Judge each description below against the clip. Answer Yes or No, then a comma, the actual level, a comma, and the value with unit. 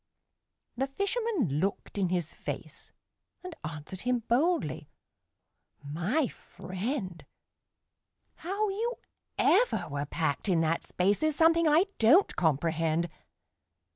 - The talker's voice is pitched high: Yes, high, 210 Hz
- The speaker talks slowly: Yes, slow, 110 wpm